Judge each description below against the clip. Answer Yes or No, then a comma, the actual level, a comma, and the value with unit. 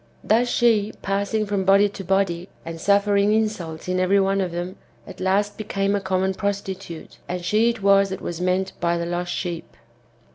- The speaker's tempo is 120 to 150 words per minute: No, average, 185 wpm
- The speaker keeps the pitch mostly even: Yes, narrow, 2.0 semitones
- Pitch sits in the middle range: No, high, 195 Hz